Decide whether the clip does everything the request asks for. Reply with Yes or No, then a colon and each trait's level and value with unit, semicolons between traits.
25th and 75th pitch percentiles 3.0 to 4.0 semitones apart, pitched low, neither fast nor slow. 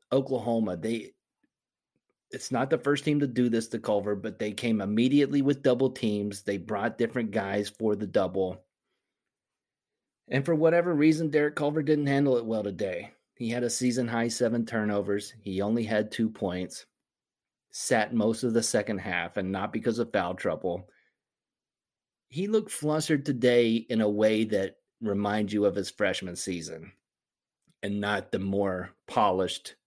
No: average, 4.5 semitones; low, 115 Hz; average, 160 wpm